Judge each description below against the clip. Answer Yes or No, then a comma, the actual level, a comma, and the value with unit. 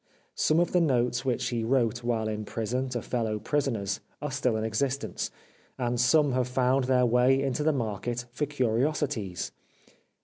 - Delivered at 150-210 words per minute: Yes, average, 165 wpm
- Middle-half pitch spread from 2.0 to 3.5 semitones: Yes, average, 2.9 semitones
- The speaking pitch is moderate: No, low, 125 Hz